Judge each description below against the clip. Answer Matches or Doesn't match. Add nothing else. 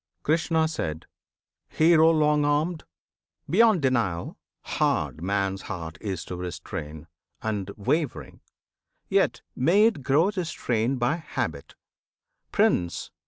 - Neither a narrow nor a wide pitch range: Doesn't match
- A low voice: Matches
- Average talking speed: Doesn't match